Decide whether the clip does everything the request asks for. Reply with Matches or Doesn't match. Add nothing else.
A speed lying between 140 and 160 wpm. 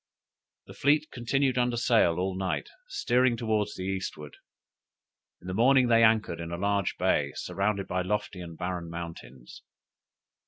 Matches